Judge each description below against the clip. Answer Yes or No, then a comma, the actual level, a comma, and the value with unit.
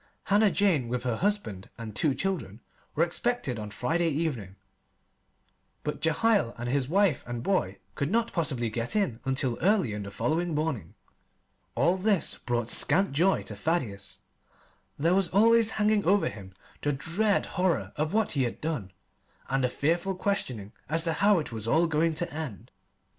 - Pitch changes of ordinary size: No, wide, 7.9 semitones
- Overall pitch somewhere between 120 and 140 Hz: No, medium, 155 Hz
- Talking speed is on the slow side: No, average, 170 wpm